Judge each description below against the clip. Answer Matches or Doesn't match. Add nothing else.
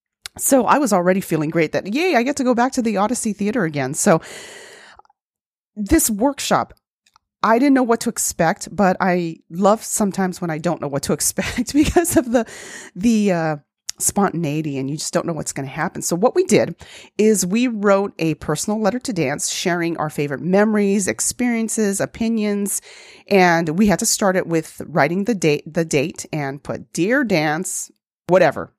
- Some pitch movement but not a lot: Doesn't match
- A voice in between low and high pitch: Doesn't match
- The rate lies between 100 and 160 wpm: Doesn't match